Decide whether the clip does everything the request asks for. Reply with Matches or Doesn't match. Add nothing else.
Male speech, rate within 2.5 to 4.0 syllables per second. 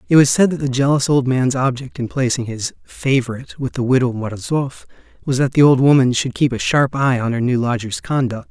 Doesn't match